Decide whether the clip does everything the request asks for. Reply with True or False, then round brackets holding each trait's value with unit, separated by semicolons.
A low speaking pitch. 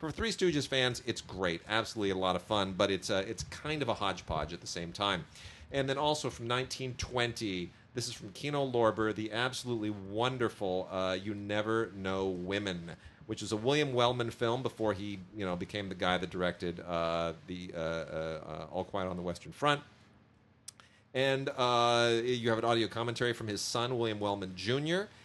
True (110 Hz)